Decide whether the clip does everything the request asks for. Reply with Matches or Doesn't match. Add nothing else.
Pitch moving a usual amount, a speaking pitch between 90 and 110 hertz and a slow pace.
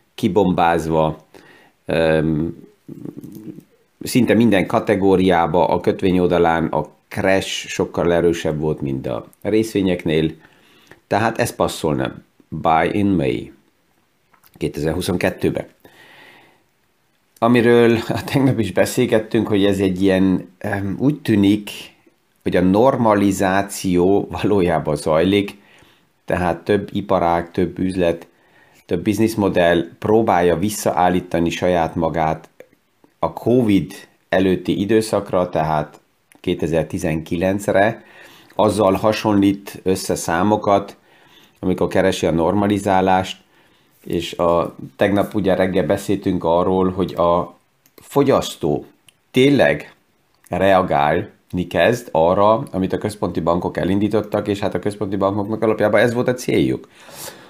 Matches